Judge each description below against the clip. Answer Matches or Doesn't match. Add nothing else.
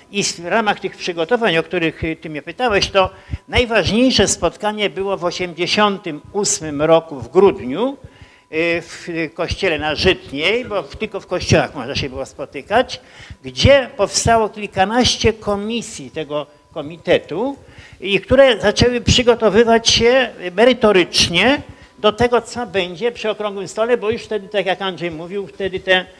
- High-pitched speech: Matches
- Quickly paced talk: Doesn't match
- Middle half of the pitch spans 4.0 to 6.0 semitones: Matches